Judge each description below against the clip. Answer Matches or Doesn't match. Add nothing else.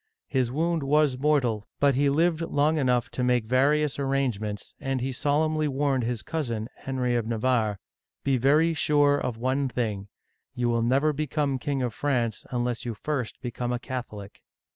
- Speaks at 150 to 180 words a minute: Matches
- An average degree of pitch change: Matches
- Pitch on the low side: Matches